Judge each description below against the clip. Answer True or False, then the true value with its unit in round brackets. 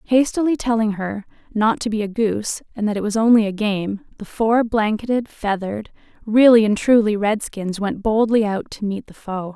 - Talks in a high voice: True (215 Hz)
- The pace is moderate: True (190 wpm)